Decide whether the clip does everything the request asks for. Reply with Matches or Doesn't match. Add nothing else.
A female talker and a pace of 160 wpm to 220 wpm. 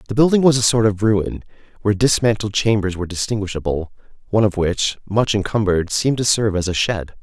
Doesn't match